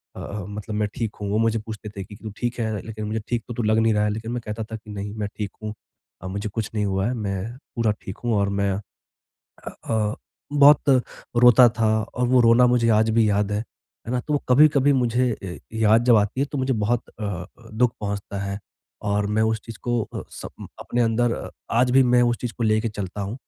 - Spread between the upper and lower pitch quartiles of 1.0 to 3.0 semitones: Yes, narrow, 2.6 semitones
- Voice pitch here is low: Yes, low, 110 Hz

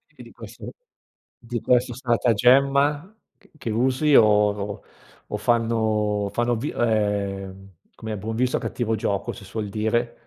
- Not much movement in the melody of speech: No, average, 3.2 semitones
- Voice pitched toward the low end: Yes, low, 115 Hz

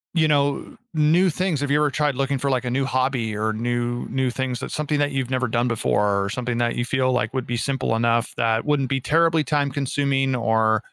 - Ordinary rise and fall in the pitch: Yes, average, 3.1 semitones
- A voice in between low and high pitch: No, low, 130 Hz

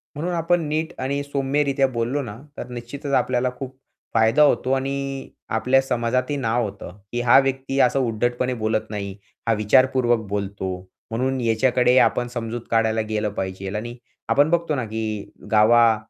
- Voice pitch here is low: Yes, low, 120 Hz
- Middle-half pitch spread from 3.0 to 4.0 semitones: Yes, average, 3.3 semitones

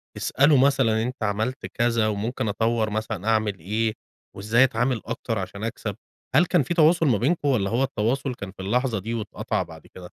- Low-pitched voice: Yes, low, 115 Hz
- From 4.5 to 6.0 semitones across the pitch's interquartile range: No, average, 3.7 semitones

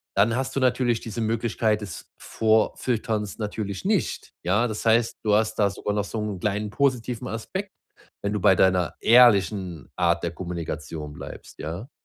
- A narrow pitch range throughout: No, average, 3.4 semitones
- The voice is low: Yes, low, 105 Hz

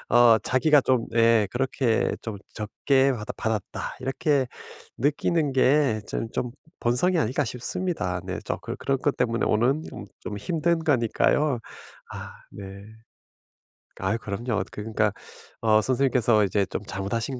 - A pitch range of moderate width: Yes, average, 4.3 semitones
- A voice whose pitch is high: No, low, 120 Hz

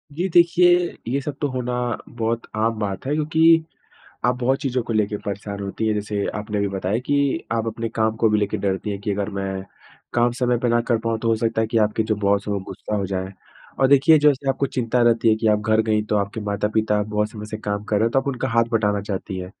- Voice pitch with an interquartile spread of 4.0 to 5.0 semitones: No, average, 3.3 semitones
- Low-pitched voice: Yes, low, 110 Hz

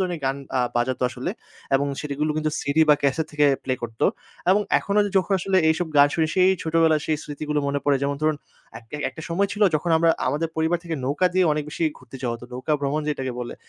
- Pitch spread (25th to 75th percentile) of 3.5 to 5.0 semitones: No, average, 3.0 semitones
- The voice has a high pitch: No, medium, 150 Hz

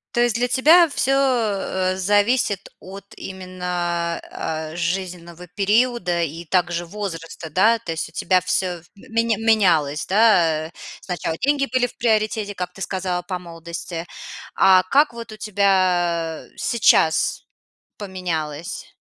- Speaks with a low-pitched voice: No, medium, 185 Hz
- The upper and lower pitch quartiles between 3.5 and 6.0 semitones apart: Yes, average, 4.2 semitones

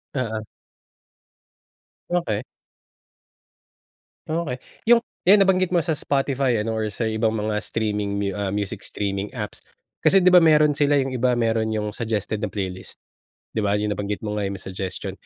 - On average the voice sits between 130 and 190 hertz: No, low, 110 Hz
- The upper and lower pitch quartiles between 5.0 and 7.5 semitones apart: Yes, wide, 5.4 semitones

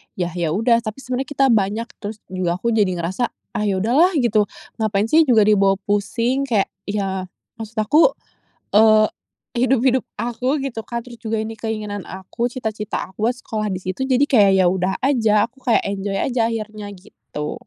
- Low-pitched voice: No, high, 220 Hz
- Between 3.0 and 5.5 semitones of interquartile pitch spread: Yes, average, 3.3 semitones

